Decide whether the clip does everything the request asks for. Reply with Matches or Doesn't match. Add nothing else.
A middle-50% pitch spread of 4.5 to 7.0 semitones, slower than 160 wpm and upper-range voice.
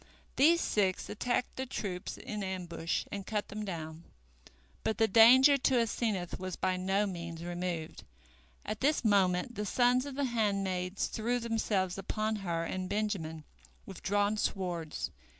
Doesn't match